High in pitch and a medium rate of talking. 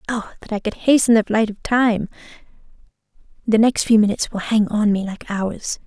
Yes: high, 215 Hz; average, 185 wpm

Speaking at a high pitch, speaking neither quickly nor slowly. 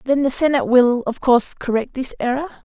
Yes: very high, 260 Hz; average, 195 wpm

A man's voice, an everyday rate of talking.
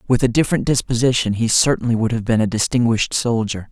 Yes: male; average, 195 wpm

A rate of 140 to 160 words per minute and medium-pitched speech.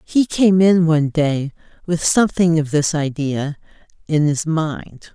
Yes: average, 150 wpm; medium, 160 Hz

